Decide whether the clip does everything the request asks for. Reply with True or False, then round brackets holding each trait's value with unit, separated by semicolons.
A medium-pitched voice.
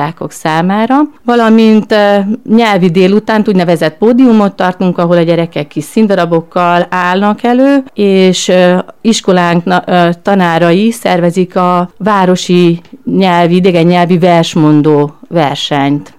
True (180 Hz)